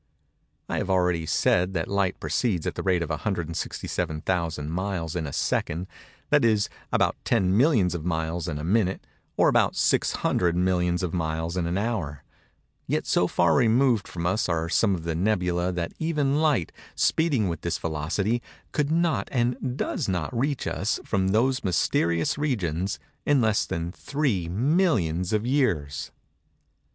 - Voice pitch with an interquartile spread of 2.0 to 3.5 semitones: No, wide, 5.6 semitones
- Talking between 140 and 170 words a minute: Yes, average, 155 wpm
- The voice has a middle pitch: No, very low, 95 Hz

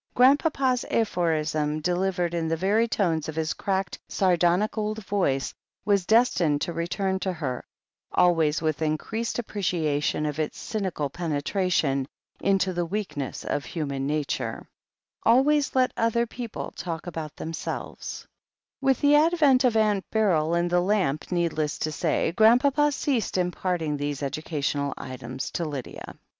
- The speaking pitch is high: No, medium, 175 Hz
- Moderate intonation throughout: No, wide, 5.8 semitones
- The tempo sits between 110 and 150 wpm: Yes, average, 145 wpm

